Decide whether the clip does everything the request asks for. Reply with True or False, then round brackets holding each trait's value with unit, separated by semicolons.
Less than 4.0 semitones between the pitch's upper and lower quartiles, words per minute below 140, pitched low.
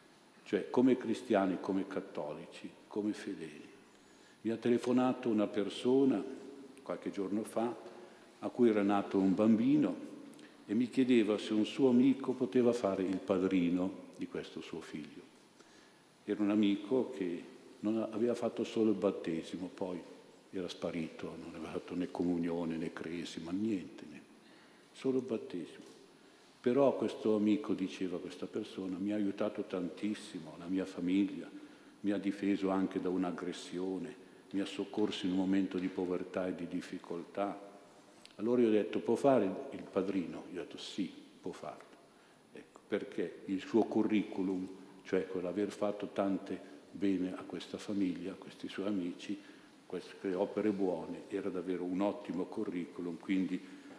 False (3.3 semitones; 145 wpm; 100 Hz)